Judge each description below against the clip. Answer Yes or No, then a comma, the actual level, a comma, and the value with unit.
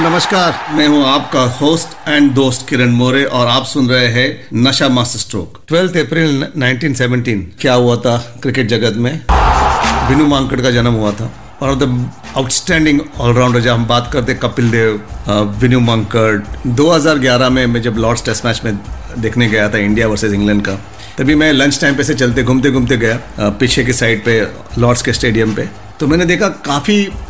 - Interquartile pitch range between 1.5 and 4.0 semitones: Yes, average, 3.4 semitones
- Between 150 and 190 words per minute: No, average, 135 wpm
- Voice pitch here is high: No, low, 125 Hz